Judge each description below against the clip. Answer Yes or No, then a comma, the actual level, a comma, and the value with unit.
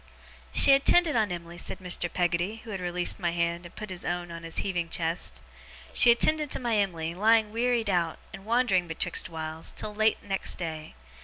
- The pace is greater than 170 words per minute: Yes, average, 200 wpm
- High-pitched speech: No, medium, 180 Hz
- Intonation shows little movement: No, average, 4.5 semitones